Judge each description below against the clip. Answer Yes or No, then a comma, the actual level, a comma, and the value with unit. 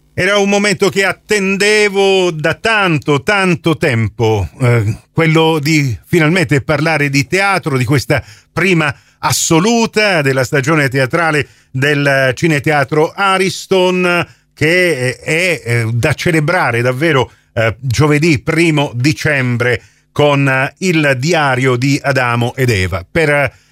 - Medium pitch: Yes, medium, 150 Hz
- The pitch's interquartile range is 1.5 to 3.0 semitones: No, average, 4.8 semitones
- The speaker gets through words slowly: Yes, slow, 110 wpm